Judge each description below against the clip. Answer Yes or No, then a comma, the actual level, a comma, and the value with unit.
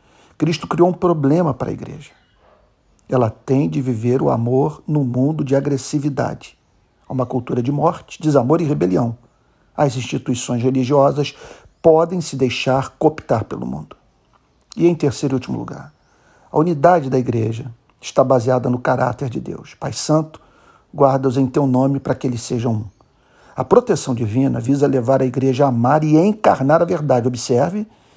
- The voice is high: No, low, 135 Hz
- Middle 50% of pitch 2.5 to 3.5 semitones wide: Yes, average, 2.9 semitones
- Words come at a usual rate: Yes, average, 160 wpm